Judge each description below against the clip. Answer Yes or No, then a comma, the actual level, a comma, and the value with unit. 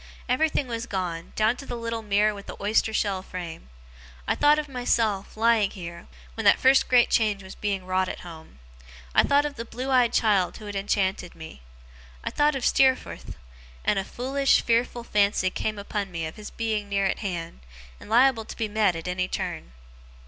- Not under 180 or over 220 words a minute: Yes, average, 195 wpm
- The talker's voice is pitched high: Yes, high, 210 Hz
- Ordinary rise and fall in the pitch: Yes, average, 4.0 semitones